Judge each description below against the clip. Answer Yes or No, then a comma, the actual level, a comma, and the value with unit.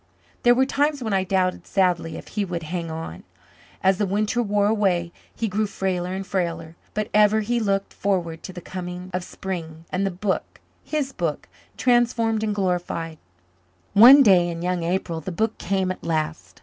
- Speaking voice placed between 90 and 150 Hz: No, high, 190 Hz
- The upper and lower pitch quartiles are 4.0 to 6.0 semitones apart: No, average, 3.5 semitones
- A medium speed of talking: Yes, average, 180 wpm